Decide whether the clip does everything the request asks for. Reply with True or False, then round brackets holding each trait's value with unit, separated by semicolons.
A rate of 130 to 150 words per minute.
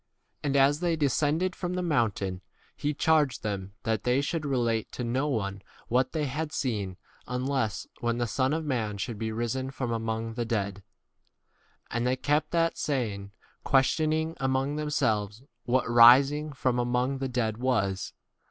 False (175 wpm)